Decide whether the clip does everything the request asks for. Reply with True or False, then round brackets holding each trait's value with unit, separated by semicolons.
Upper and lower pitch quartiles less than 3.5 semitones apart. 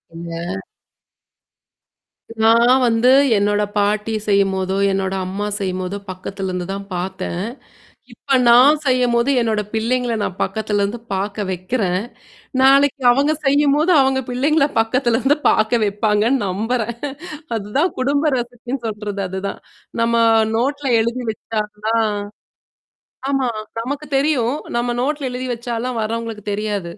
False (4.0 semitones)